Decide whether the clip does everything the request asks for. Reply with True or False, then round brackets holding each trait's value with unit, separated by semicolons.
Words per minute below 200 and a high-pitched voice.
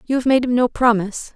False (265 wpm; 240 Hz)